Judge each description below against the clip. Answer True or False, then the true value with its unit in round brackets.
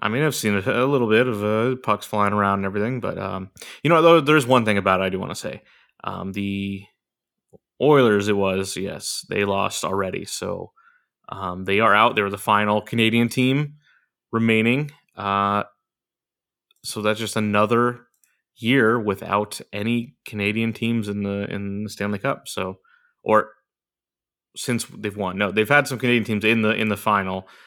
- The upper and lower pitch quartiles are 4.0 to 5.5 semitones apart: False (3.3 semitones)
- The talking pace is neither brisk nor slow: True (175 wpm)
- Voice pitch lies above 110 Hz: False (105 Hz)